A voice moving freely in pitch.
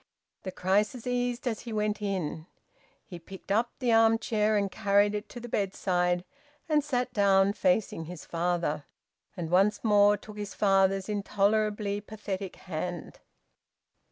No: narrow, 2.6 semitones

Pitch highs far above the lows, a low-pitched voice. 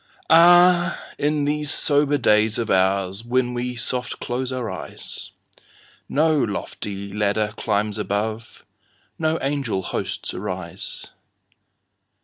Yes: wide, 5.7 semitones; low, 120 Hz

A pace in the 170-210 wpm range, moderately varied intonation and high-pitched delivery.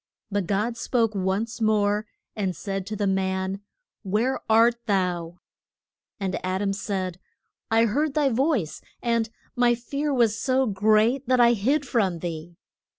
No: average, 150 wpm; average, 3.9 semitones; high, 215 Hz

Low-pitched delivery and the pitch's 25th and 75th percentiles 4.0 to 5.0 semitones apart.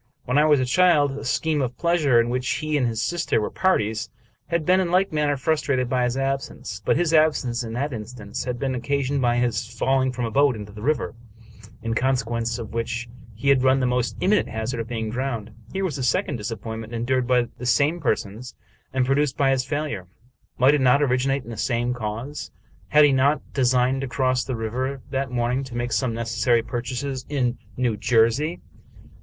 No: low, 125 Hz; average, 3.2 semitones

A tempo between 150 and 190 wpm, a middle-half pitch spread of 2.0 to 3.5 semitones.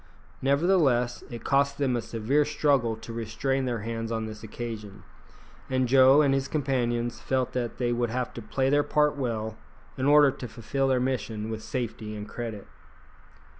Yes: average, 170 wpm; average, 3.1 semitones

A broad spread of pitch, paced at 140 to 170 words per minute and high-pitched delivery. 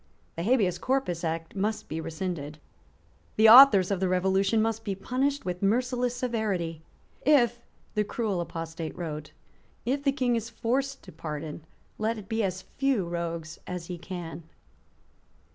Yes: wide, 5.9 semitones; average, 150 wpm; high, 195 Hz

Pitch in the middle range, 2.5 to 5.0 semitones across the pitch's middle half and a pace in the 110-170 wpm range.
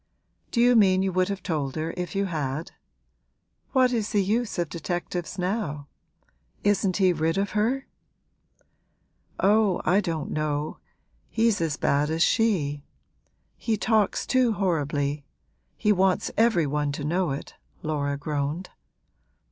No: medium, 180 Hz; wide, 5.4 semitones; average, 140 wpm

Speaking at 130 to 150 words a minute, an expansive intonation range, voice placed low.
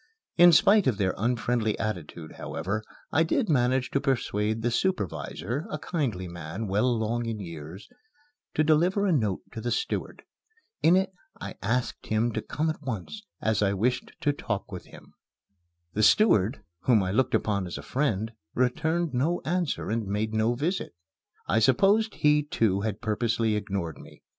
No: average, 165 wpm; wide, 6.2 semitones; low, 115 Hz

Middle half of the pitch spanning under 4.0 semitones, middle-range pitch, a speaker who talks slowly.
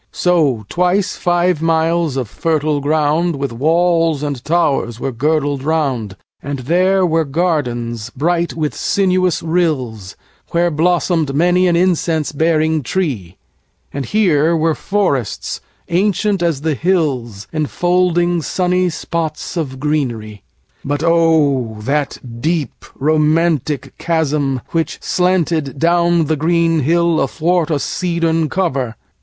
Yes: average, 3.6 semitones; medium, 160 Hz; slow, 105 wpm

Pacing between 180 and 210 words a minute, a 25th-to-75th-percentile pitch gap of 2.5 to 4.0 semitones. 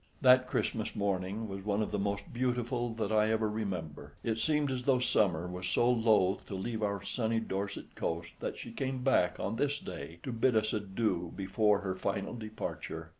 Yes: average, 190 wpm; average, 3.7 semitones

